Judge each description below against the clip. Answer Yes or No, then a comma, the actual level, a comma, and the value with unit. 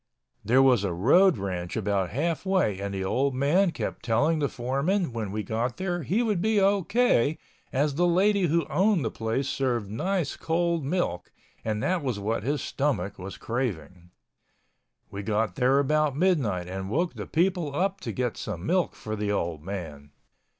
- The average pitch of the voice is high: No, low, 135 Hz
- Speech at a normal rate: Yes, average, 180 wpm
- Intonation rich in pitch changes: Yes, wide, 9.0 semitones